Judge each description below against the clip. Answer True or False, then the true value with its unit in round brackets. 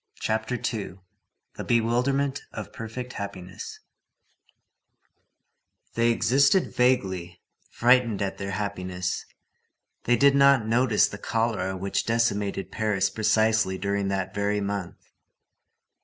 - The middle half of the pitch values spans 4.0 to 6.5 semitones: False (3.6 semitones)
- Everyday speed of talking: False (100 wpm)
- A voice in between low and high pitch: False (110 Hz)